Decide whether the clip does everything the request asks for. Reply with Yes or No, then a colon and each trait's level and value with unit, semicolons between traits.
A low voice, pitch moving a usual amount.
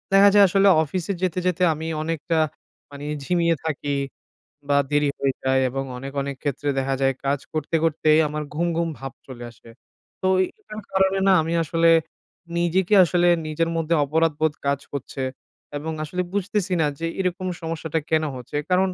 No: medium, 160 Hz; average, 3.9 semitones